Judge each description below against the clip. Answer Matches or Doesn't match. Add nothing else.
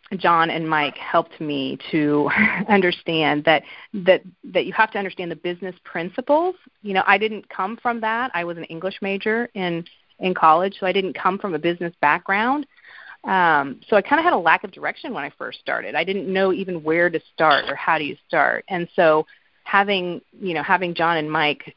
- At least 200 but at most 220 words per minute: Matches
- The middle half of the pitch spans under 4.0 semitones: Matches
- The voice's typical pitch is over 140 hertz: Matches